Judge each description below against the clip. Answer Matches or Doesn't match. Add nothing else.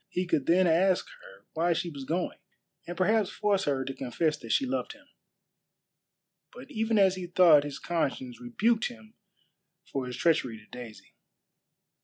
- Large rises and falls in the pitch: Matches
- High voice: Doesn't match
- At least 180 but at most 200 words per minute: Doesn't match